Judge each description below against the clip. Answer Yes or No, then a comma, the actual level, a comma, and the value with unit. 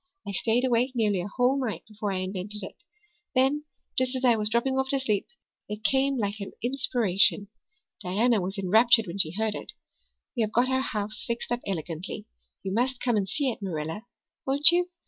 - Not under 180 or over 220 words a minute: Yes, average, 195 wpm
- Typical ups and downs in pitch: Yes, average, 4.4 semitones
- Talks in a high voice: Yes, high, 225 Hz